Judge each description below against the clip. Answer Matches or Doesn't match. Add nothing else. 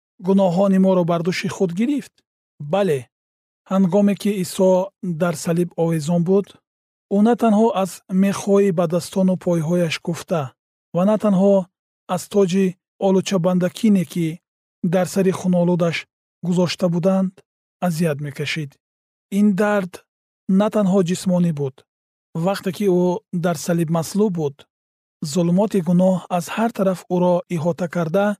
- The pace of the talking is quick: Doesn't match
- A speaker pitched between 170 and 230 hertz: Matches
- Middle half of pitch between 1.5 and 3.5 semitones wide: Matches